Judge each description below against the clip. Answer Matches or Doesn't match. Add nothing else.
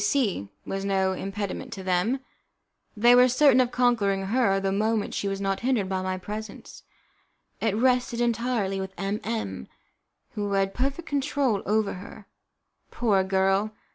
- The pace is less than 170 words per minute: Matches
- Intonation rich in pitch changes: Doesn't match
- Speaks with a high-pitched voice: Matches